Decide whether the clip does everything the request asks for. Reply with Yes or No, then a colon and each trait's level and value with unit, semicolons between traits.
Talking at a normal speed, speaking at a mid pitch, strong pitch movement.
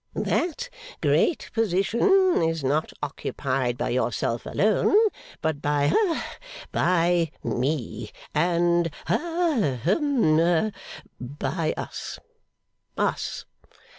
No: slow, 85 wpm; medium, 170 Hz; wide, 8.0 semitones